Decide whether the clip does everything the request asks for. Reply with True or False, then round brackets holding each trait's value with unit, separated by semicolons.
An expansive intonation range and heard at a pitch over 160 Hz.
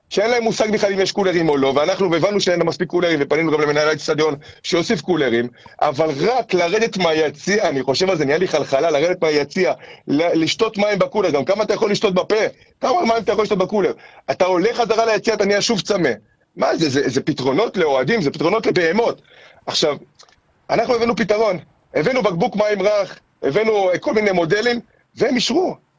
True (5.9 semitones; 190 Hz)